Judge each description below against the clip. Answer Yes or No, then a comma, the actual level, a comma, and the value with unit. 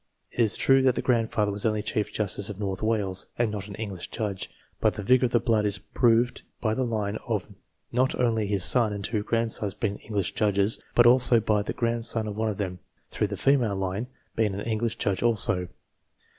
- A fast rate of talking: Yes, fast, 210 wpm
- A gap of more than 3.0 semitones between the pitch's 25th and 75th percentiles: No, narrow, 2.4 semitones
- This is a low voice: Yes, low, 110 Hz